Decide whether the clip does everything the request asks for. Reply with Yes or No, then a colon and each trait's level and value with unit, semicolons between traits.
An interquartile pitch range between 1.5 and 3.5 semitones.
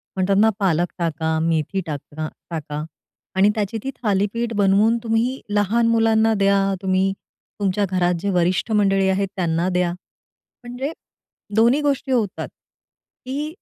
No: average, 3.9 semitones